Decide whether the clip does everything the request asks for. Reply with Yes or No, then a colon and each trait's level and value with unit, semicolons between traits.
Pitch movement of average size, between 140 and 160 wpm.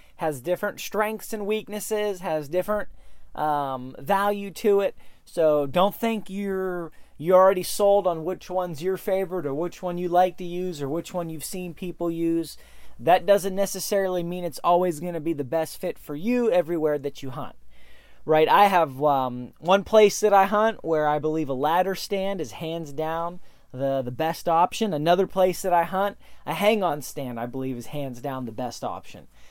No: average, 4.4 semitones; average, 190 wpm